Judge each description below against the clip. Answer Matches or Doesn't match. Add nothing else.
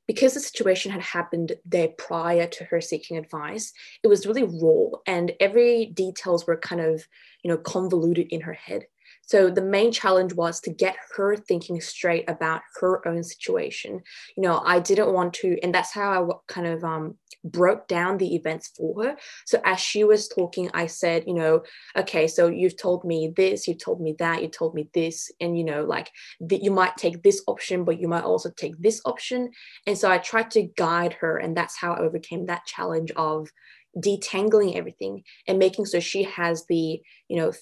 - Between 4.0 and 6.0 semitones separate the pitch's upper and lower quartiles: Doesn't match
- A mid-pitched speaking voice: Matches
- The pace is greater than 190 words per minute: Matches